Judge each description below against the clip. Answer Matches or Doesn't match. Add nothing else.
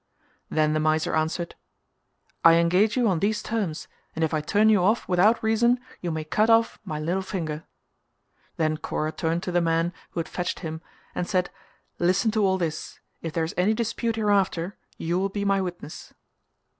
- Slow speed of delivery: Doesn't match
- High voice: Doesn't match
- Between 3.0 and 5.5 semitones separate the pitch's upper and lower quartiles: Matches